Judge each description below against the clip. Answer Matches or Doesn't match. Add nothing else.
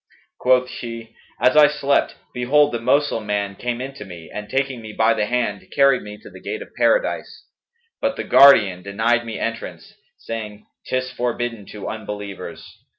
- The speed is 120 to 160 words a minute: Doesn't match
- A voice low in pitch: Matches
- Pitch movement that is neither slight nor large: Matches